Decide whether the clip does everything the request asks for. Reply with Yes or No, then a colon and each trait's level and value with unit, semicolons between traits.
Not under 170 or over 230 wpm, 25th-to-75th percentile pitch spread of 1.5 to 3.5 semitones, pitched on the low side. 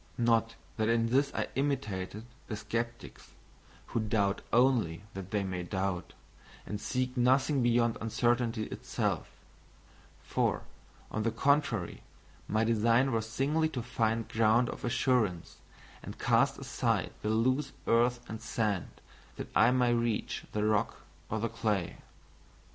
No: slow, 135 wpm; narrow, 2.5 semitones; low, 115 Hz